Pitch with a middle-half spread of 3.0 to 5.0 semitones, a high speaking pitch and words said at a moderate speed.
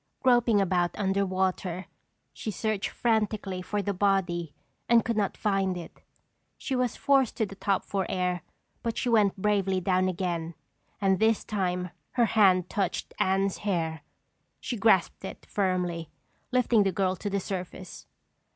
No: narrow, 2.6 semitones; high, 195 Hz; average, 150 wpm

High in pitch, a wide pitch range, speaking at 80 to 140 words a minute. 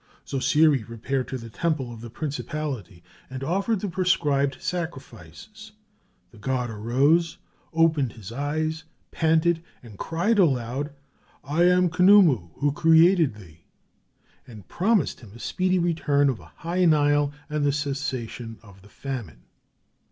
No: medium, 145 Hz; wide, 5.9 semitones; slow, 135 wpm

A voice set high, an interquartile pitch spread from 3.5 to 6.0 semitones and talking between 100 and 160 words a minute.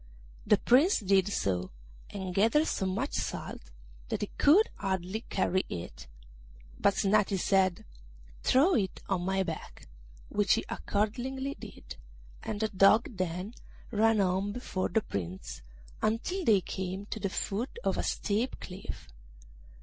No: high, 200 Hz; average, 3.1 semitones; average, 140 wpm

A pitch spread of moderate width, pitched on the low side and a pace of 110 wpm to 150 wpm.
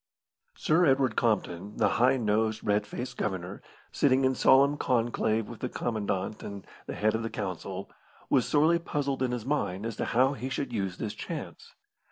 No: average, 4.1 semitones; low, 115 Hz; average, 180 wpm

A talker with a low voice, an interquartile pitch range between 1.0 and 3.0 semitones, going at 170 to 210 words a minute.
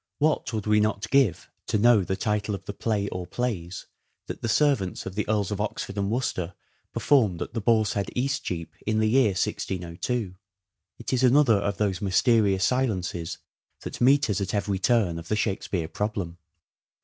No: low, 105 Hz; average, 3.7 semitones; average, 180 wpm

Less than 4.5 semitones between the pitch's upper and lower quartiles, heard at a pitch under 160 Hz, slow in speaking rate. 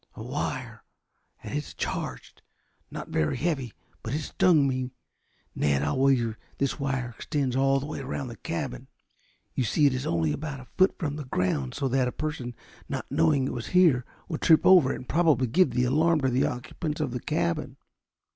No: average, 3.6 semitones; low, 135 Hz; average, 195 wpm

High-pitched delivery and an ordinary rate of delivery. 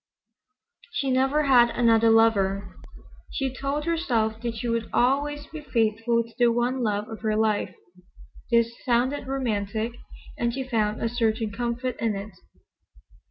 Yes: high, 235 Hz; average, 145 wpm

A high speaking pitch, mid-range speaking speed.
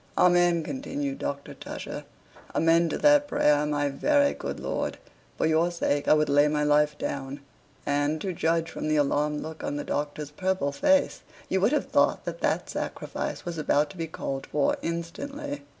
No: medium, 155 Hz; average, 180 wpm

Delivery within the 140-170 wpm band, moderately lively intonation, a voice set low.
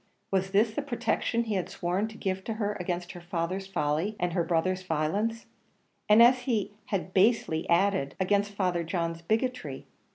No: average, 165 wpm; average, 3.9 semitones; high, 190 Hz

